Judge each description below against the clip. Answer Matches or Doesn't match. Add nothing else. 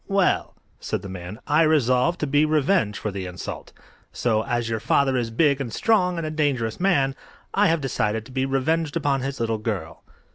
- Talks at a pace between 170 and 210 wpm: Matches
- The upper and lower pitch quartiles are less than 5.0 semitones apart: Doesn't match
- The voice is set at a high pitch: Doesn't match